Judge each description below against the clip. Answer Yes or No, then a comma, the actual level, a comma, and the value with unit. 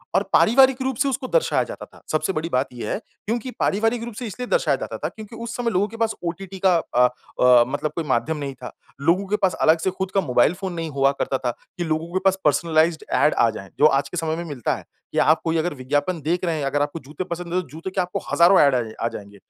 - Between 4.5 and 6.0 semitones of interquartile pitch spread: Yes, average, 5.1 semitones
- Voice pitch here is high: No, medium, 170 Hz